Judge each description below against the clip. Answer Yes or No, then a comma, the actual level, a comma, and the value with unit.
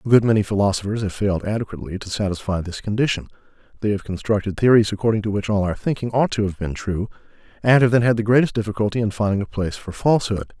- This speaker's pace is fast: Yes, fast, 220 wpm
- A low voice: Yes, low, 105 Hz